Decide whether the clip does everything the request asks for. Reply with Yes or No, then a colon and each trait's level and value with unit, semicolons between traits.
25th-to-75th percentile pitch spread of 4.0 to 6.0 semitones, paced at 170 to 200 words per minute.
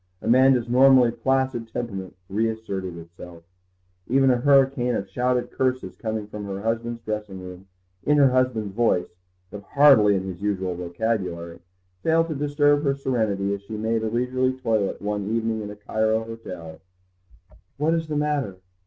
No: average, 4.5 semitones; average, 155 wpm